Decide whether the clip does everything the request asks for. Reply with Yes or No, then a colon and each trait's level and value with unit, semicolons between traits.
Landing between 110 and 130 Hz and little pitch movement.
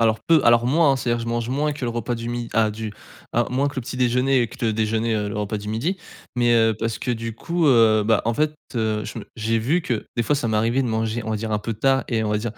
Yes: low, 115 Hz; narrow, 2.3 semitones